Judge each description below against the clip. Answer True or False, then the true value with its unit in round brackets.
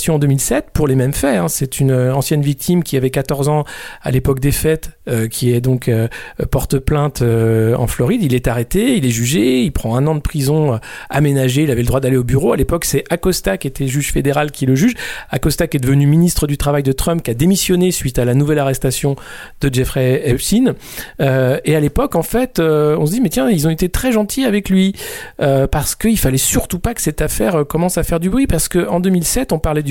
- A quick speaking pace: True (240 wpm)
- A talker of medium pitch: True (145 Hz)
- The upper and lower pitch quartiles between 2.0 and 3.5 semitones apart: False (4.4 semitones)